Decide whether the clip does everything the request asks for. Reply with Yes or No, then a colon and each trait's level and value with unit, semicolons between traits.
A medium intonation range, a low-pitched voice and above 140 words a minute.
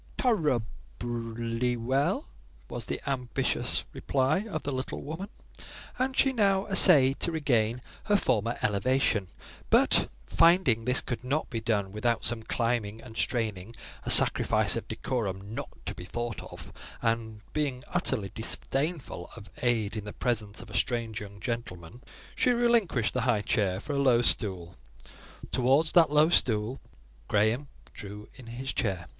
Yes: average, 4.6 semitones; low, 120 Hz; average, 150 wpm